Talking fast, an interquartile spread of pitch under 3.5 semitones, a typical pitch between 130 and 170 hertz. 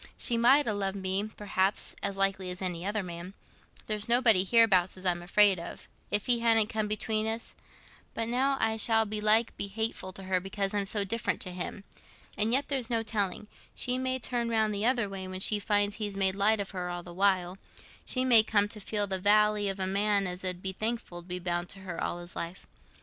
No: fast, 215 wpm; average, 2.9 semitones; high, 205 Hz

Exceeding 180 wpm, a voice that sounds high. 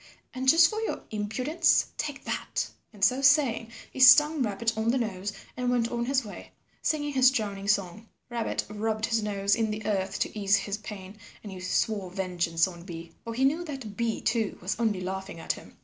Yes: average, 200 wpm; high, 220 Hz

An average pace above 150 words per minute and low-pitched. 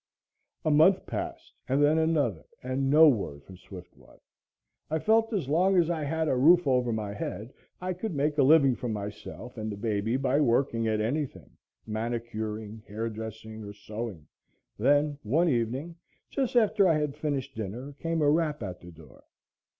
Yes: average, 170 wpm; low, 130 Hz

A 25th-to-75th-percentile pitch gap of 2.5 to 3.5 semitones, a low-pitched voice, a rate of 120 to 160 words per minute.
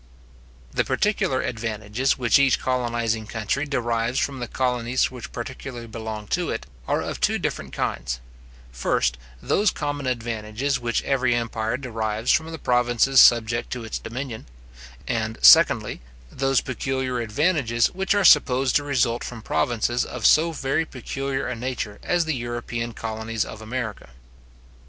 Yes: average, 3.0 semitones; low, 120 Hz; average, 145 wpm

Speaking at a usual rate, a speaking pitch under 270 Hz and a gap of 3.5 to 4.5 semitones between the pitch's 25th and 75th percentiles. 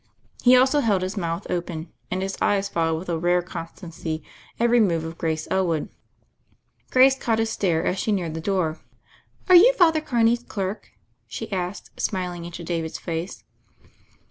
No: average, 170 wpm; medium, 185 Hz; average, 5.1 semitones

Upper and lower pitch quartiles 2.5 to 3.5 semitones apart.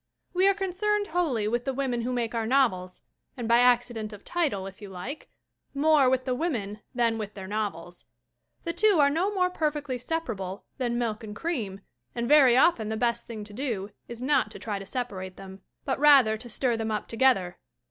No: average, 5.2 semitones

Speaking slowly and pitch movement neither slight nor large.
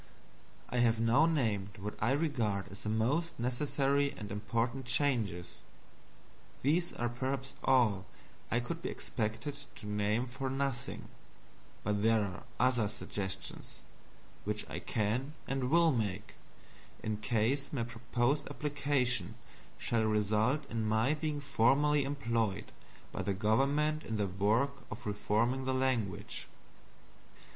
Yes: slow, 130 wpm; average, 4.5 semitones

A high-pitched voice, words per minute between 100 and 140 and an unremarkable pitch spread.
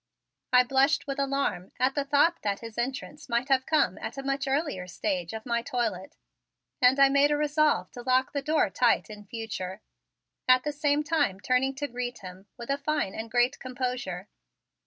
No: very high, 255 Hz; average, 190 wpm; average, 4.1 semitones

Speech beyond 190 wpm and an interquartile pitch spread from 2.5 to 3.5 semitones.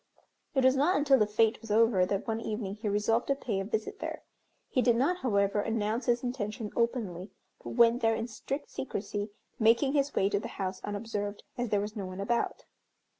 Yes: fast, 205 wpm; average, 3.0 semitones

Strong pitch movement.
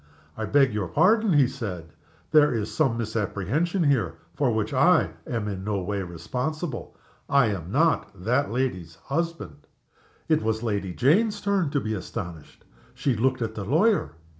Yes: wide, 6.7 semitones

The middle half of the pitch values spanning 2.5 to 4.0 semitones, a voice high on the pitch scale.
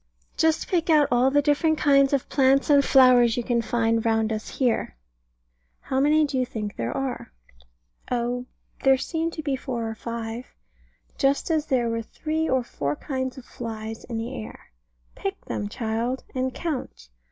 Yes: average, 3.6 semitones; very high, 255 Hz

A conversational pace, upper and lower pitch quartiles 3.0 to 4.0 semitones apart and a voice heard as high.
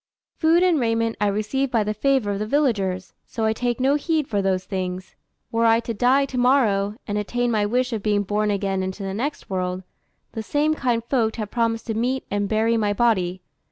No: fast, 215 wpm; average, 3.5 semitones; high, 225 Hz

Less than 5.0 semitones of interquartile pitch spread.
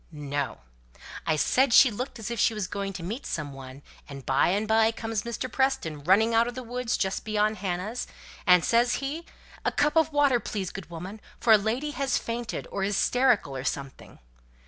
No: average, 5.3 semitones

